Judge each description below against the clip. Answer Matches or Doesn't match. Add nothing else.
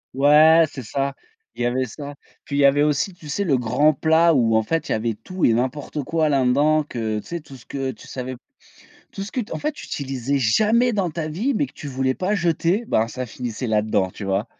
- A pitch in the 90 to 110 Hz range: Doesn't match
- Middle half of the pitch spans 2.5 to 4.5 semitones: Doesn't match